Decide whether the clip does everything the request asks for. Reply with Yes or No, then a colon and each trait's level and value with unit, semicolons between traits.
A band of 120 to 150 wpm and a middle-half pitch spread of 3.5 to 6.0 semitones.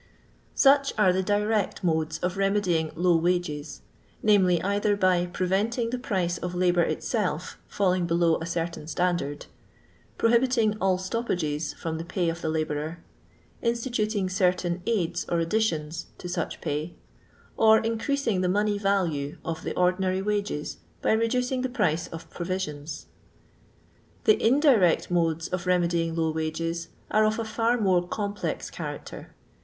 Yes: average, 140 wpm; average, 4.2 semitones